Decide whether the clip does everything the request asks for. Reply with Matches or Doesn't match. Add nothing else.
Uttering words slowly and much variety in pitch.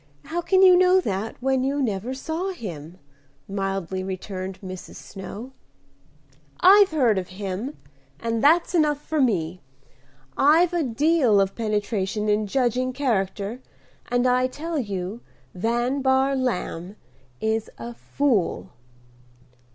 Matches